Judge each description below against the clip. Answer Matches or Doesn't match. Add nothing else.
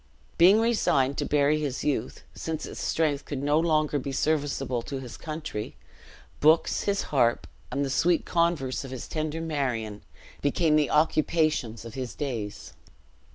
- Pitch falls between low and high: Matches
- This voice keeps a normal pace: Matches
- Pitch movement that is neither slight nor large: Matches